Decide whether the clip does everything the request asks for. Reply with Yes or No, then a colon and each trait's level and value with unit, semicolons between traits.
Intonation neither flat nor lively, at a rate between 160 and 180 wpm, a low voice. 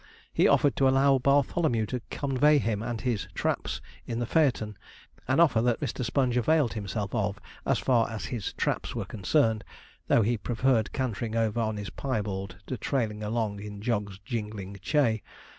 Yes: average, 3.8 semitones; average, 170 wpm; low, 115 Hz